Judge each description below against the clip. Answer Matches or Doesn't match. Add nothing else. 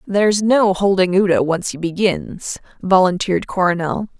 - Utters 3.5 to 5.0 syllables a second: Matches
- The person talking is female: Matches